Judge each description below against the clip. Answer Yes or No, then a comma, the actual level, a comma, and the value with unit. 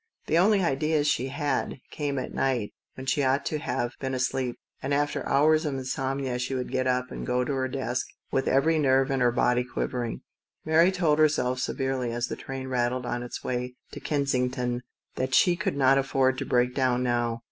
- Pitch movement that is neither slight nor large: No, narrow, 2.0 semitones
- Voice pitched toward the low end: Yes, low, 130 Hz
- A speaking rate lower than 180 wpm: No, average, 200 wpm